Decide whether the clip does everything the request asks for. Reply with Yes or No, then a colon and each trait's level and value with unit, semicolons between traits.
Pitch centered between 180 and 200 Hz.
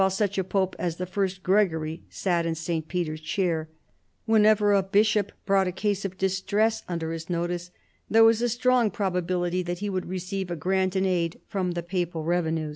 Yes: medium, 185 Hz